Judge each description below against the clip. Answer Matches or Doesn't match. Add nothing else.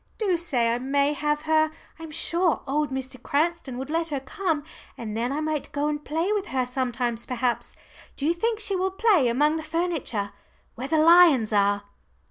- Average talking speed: Matches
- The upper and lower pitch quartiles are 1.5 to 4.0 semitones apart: Doesn't match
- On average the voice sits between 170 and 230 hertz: Doesn't match